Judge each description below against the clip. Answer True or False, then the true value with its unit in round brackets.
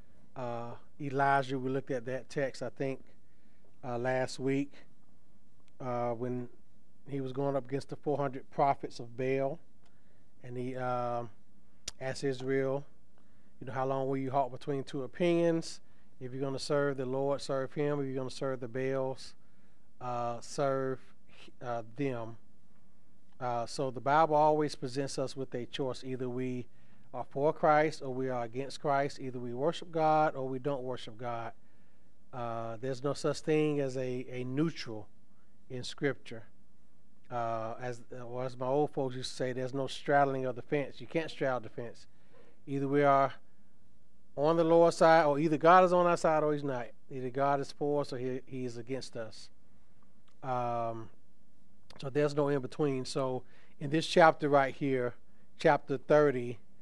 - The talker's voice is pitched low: True (130 Hz)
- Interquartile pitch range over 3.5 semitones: False (2.7 semitones)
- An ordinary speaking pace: True (170 wpm)